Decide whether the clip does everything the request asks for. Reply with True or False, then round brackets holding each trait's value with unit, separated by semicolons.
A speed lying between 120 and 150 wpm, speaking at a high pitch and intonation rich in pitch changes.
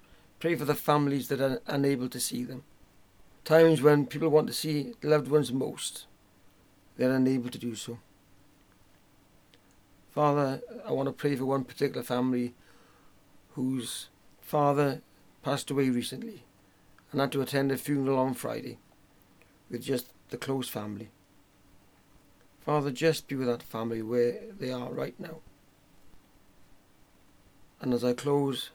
False (140 wpm; 125 Hz; 6.4 semitones)